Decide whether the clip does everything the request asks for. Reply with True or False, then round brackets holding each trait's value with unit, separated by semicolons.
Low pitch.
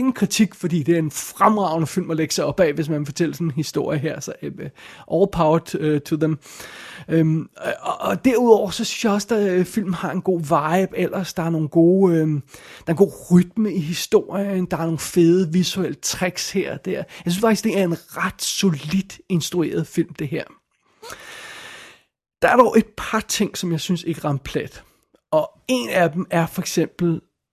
False (180 Hz)